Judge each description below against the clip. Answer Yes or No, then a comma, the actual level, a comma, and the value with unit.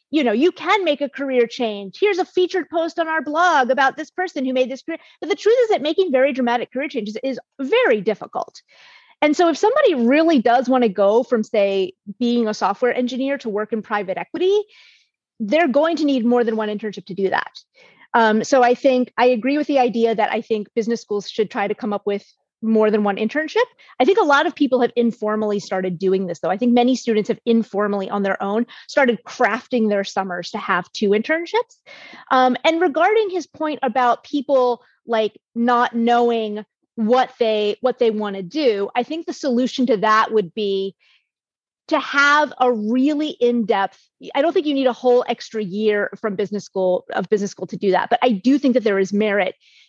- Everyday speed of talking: No, fast, 210 wpm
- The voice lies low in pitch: No, high, 245 Hz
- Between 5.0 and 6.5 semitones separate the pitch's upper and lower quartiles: Yes, wide, 5.6 semitones